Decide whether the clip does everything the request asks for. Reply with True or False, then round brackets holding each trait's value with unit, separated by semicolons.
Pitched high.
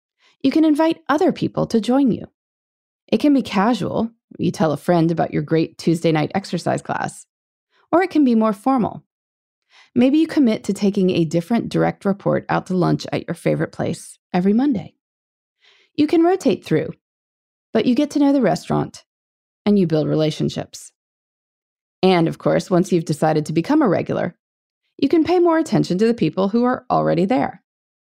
True (210 Hz)